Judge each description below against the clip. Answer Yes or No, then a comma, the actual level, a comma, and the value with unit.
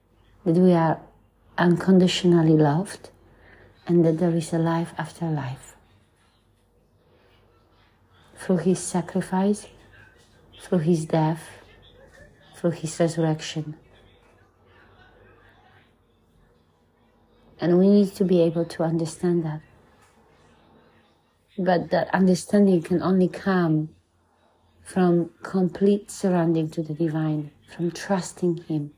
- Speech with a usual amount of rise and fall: No, wide, 8.1 semitones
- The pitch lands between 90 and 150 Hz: No, medium, 165 Hz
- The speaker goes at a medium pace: No, slow, 95 wpm